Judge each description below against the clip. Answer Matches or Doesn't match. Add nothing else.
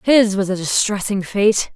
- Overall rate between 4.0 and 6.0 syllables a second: Matches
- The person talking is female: Matches